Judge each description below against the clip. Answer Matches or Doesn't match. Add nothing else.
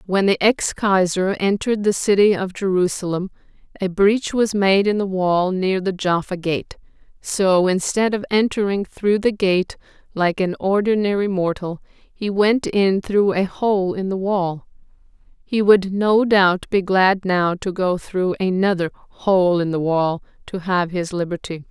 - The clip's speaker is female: Matches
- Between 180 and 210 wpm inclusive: Doesn't match